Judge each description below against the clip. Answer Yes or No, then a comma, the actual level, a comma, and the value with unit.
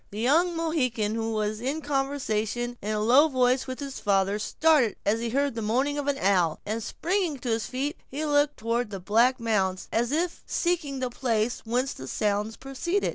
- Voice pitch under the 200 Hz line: No, high, 245 Hz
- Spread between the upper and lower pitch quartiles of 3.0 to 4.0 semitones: No, average, 4.8 semitones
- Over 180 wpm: Yes, average, 190 wpm